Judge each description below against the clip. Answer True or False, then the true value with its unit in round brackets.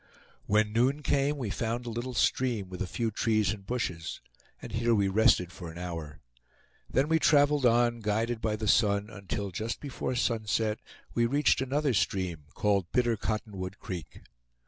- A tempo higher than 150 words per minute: True (170 wpm)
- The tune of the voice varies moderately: True (3.7 semitones)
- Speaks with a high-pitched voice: False (110 Hz)